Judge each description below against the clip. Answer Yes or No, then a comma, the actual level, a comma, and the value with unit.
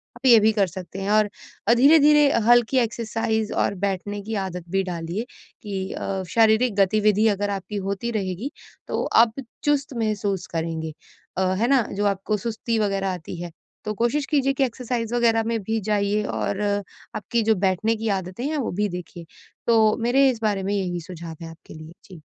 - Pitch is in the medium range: No, high, 210 Hz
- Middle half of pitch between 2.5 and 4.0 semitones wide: Yes, average, 3.3 semitones